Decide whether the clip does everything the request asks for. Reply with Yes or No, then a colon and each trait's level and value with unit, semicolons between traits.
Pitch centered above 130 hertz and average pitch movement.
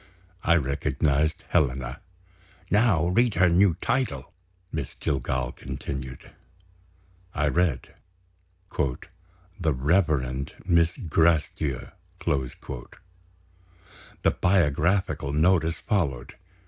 No: very low, 80 Hz; average, 4.6 semitones